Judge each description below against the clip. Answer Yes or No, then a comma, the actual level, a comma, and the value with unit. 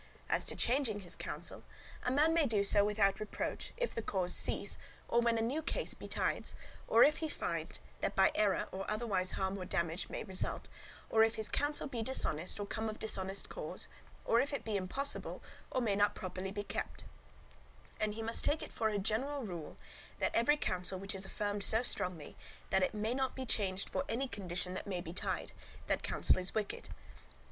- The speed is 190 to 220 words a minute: Yes, average, 200 wpm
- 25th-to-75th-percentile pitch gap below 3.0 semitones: No, average, 3.8 semitones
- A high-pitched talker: Yes, high, 210 Hz